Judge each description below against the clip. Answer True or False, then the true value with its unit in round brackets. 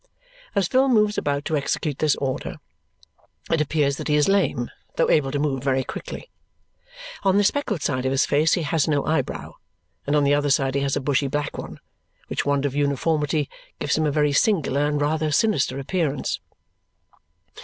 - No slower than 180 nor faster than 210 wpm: True (185 wpm)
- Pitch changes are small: True (2.3 semitones)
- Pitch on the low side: False (145 Hz)